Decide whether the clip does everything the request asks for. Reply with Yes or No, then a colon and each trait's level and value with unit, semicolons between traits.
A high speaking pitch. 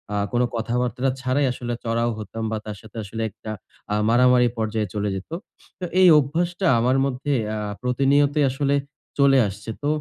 No: low, 125 Hz